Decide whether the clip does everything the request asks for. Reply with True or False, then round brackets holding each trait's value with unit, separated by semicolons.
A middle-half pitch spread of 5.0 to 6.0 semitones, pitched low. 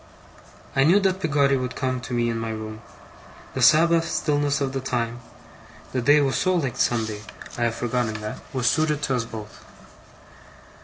False (4.0 semitones; 130 Hz)